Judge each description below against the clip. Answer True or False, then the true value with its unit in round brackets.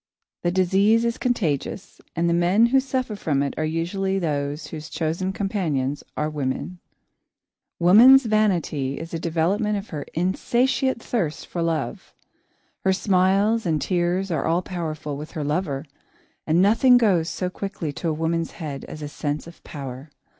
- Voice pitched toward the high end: False (175 Hz)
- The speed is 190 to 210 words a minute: False (160 wpm)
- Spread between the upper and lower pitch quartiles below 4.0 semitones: False (4.5 semitones)